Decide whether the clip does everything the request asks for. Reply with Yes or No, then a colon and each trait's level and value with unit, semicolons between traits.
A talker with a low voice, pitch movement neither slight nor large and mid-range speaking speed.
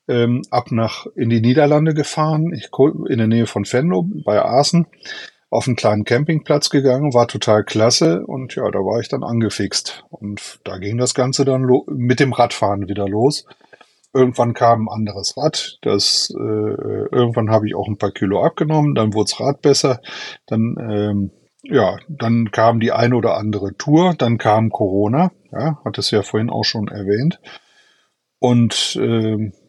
Yes: low, 115 Hz; average, 4.7 semitones; average, 170 wpm